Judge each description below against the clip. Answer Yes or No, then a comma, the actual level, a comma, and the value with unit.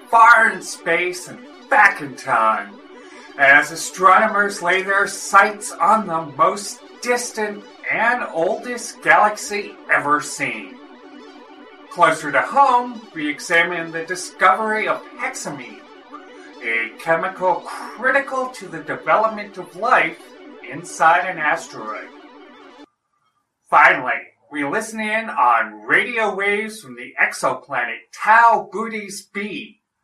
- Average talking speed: No, slow, 110 wpm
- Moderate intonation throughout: Yes, average, 4.2 semitones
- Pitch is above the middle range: Yes, high, 205 Hz